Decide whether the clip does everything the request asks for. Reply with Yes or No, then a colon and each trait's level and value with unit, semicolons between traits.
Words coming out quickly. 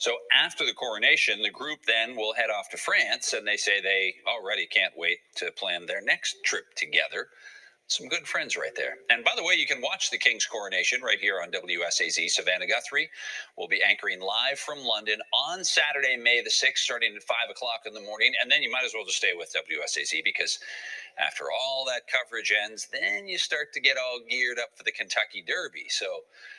Yes: fast, 210 wpm